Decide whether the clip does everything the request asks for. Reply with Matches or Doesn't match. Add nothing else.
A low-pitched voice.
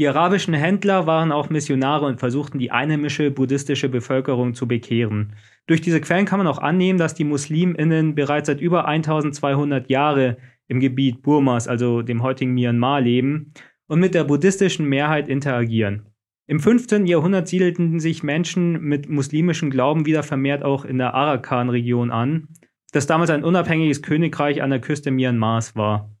Doesn't match